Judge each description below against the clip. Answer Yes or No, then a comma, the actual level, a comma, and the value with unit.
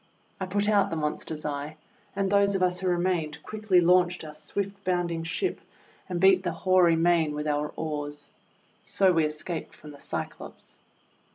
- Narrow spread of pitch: No, average, 3.4 semitones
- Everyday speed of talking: Yes, average, 170 wpm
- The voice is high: No, medium, 175 Hz